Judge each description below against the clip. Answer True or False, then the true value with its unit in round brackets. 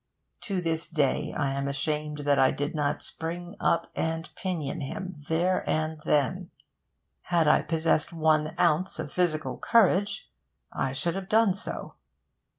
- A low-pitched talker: False (160 Hz)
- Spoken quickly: False (150 wpm)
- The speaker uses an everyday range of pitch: True (3.2 semitones)